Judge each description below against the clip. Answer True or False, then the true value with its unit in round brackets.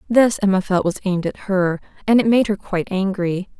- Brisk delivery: True (215 wpm)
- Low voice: False (195 Hz)